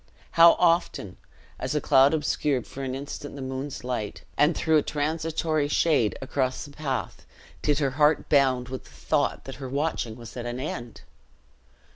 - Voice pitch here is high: No, medium, 140 Hz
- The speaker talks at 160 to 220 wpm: Yes, average, 170 wpm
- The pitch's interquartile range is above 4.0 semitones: No, average, 3.0 semitones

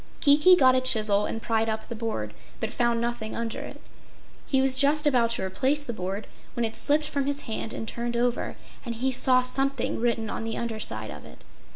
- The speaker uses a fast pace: Yes, fast, 210 wpm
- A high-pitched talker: Yes, high, 235 Hz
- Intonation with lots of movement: No, average, 3.1 semitones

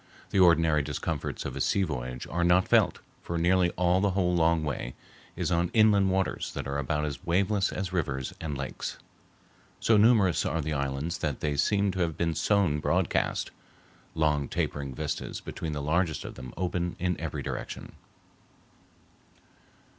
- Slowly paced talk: No, average, 165 wpm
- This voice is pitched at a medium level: No, very low, 85 Hz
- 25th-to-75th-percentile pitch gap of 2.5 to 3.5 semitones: No, average, 4.0 semitones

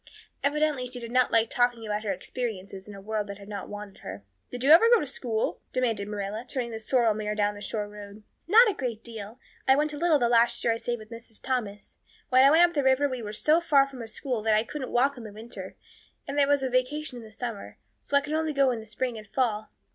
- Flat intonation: No, average, 4.3 semitones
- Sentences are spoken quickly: Yes, fast, 255 wpm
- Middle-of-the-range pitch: No, high, 240 Hz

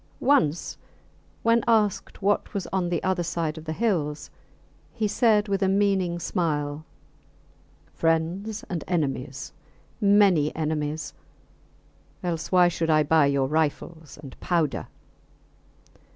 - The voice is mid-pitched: Yes, medium, 170 Hz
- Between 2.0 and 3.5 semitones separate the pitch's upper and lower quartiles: No, average, 4.0 semitones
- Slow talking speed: Yes, slow, 120 wpm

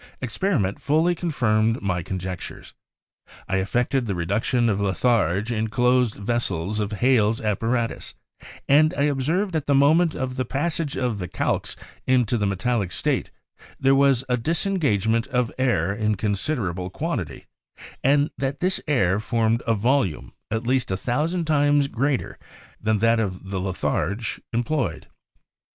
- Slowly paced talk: No, average, 145 wpm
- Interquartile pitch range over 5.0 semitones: Yes, wide, 5.4 semitones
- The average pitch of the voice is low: Yes, low, 120 Hz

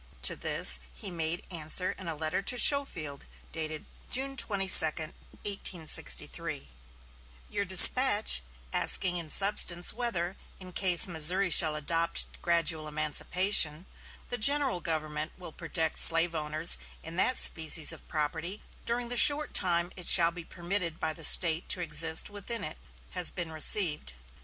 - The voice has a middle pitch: Yes, medium, 170 Hz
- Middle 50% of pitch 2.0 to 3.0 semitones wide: No, average, 3.7 semitones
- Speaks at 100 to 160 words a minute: Yes, average, 140 wpm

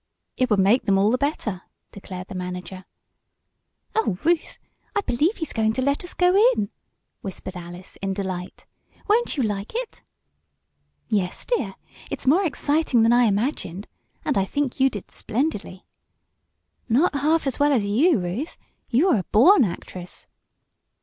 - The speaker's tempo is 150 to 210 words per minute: Yes, average, 155 wpm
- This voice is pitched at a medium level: No, high, 230 Hz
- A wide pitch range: Yes, wide, 7.4 semitones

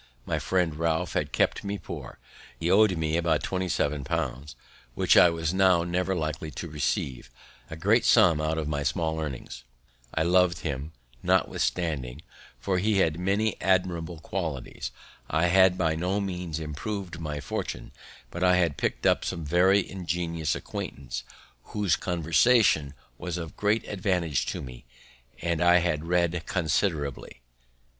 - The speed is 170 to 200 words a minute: No, average, 150 wpm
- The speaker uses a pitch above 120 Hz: No, very low, 85 Hz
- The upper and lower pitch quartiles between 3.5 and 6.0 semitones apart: No, average, 2.9 semitones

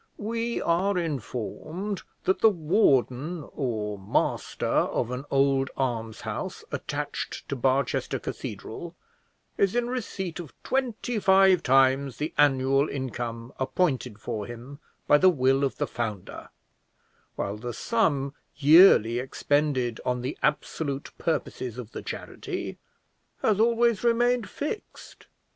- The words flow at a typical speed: No, slow, 120 wpm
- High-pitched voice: No, medium, 140 Hz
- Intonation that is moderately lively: No, wide, 7.2 semitones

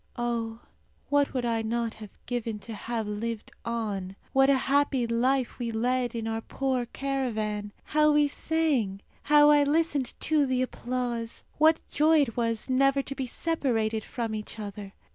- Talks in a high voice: Yes, high, 240 Hz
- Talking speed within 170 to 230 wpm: No, average, 160 wpm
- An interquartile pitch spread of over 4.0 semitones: No, average, 3.6 semitones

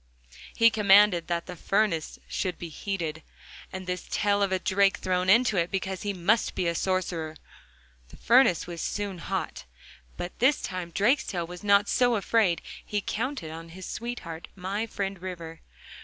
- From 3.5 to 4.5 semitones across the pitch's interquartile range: No, average, 3.1 semitones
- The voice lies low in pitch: No, high, 190 Hz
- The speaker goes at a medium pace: Yes, average, 165 wpm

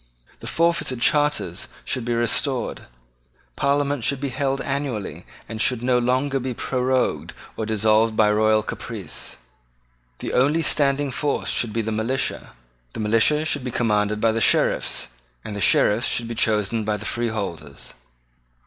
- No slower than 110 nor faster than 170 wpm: Yes, average, 150 wpm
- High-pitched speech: No, low, 120 Hz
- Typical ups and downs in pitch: Yes, average, 4.0 semitones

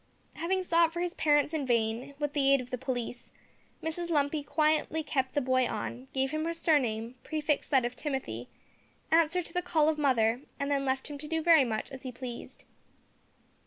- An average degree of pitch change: Yes, average, 3.8 semitones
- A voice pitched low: No, very high, 285 Hz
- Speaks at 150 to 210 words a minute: Yes, average, 200 wpm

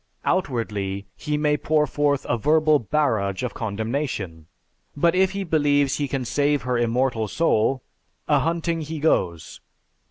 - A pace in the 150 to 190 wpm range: No, slow, 135 wpm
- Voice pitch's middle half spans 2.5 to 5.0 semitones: No, wide, 5.4 semitones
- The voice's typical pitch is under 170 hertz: Yes, medium, 140 Hz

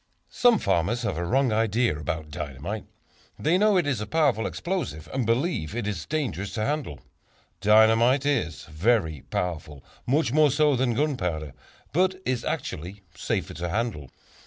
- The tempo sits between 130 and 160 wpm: Yes, average, 155 wpm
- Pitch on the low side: Yes, low, 115 Hz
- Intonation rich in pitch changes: Yes, wide, 8.7 semitones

